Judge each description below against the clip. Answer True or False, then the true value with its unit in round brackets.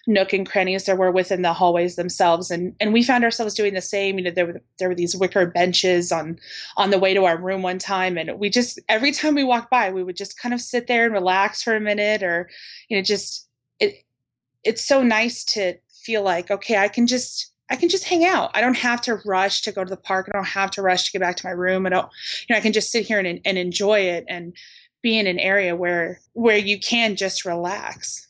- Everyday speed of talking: False (255 wpm)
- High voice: True (195 Hz)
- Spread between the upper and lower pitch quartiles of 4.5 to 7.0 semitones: False (3.7 semitones)